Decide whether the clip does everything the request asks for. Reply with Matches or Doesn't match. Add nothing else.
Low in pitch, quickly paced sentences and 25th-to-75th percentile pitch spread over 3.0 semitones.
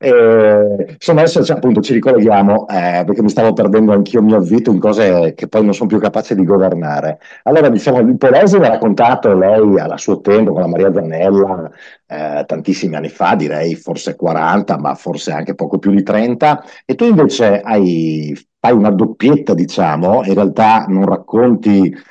Doesn't match